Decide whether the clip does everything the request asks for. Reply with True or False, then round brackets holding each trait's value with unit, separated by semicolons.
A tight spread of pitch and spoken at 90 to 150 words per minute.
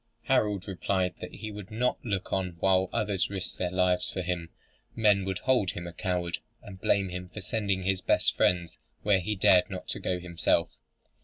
False (2.2 semitones; 185 wpm)